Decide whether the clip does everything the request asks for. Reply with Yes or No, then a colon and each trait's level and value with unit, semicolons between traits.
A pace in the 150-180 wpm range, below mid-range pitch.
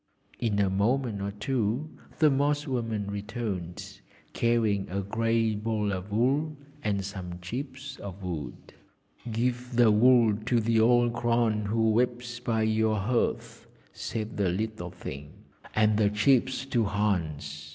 No: average, 140 wpm; low, 110 Hz